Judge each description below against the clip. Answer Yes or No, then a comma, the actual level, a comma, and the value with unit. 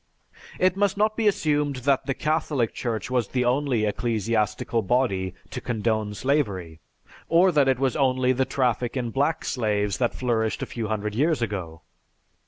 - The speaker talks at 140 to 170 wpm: Yes, average, 165 wpm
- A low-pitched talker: Yes, low, 125 Hz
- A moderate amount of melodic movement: Yes, average, 4.6 semitones